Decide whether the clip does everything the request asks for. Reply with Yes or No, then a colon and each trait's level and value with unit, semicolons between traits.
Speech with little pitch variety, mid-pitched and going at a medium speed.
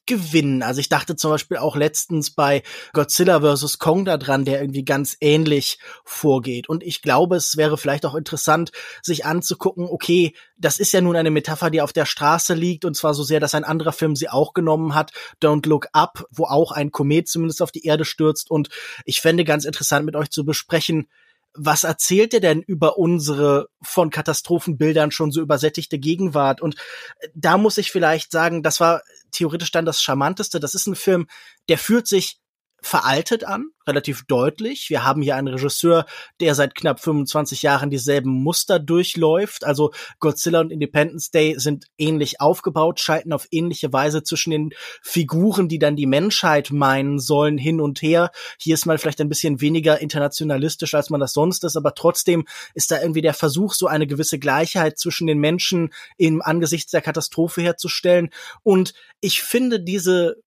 Yes: narrow, 2.3 semitones; medium, 155 Hz; average, 180 wpm